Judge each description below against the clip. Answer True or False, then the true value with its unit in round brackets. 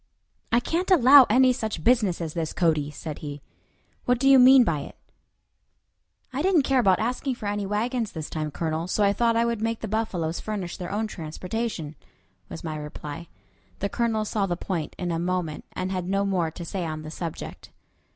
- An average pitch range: False (6.1 semitones)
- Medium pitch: False (195 Hz)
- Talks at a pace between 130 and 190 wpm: False (200 wpm)